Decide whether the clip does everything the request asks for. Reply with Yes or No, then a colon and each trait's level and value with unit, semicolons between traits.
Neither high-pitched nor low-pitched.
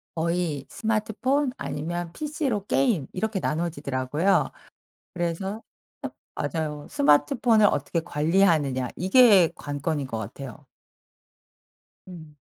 Yes: medium, 170 Hz